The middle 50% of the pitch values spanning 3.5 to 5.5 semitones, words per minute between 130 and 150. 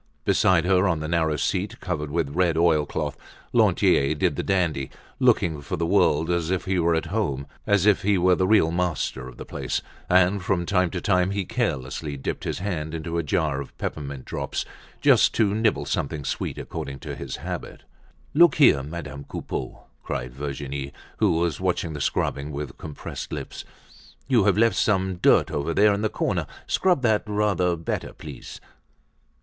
No: average, 4.5 semitones; average, 180 wpm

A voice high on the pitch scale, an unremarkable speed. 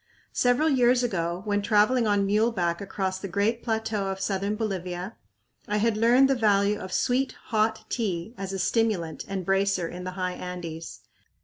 Yes: high, 200 Hz; average, 170 wpm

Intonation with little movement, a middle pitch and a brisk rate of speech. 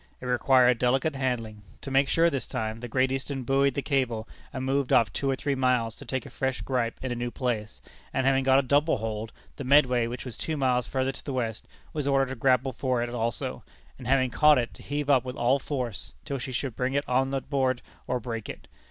No: narrow, 2.1 semitones; low, 130 Hz; fast, 235 wpm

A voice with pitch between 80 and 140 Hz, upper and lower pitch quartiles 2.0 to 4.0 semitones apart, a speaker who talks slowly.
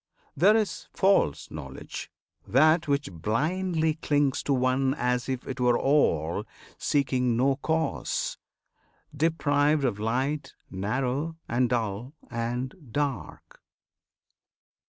Yes: low, 135 Hz; average, 3.7 semitones; slow, 100 wpm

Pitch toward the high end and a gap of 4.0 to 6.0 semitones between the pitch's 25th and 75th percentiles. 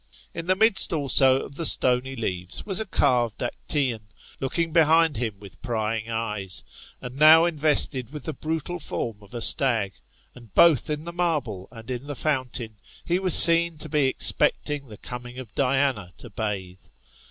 No: low, 130 Hz; wide, 5.6 semitones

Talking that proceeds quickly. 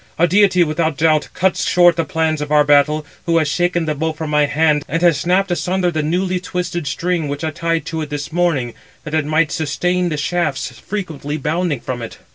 Yes: fast, 215 wpm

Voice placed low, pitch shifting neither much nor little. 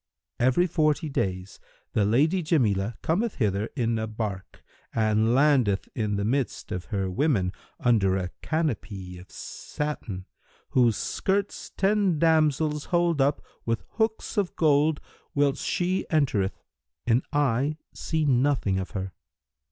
No: low, 130 Hz; wide, 7.1 semitones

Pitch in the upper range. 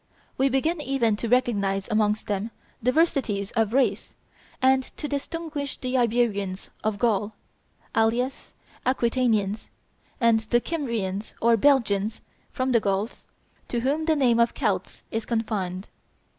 Yes: high, 235 Hz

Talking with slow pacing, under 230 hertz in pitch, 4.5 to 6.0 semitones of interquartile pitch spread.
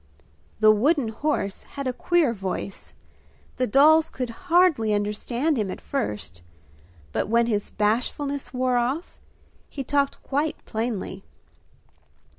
No: slow, 120 wpm; very high, 250 Hz; average, 5.1 semitones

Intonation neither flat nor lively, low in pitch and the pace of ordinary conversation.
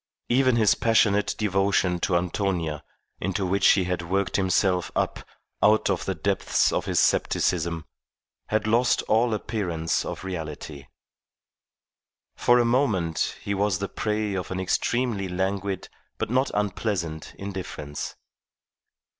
No: average, 3.2 semitones; very low, 95 Hz; slow, 130 wpm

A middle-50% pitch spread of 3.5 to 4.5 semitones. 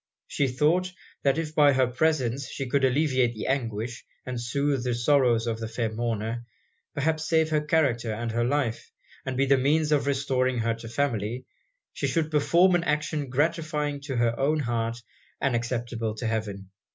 Yes: average, 4.0 semitones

